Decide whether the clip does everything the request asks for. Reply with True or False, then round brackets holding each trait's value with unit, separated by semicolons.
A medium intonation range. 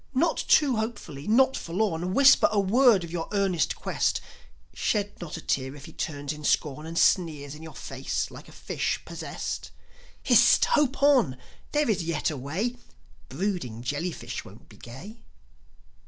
False (6.7 semitones)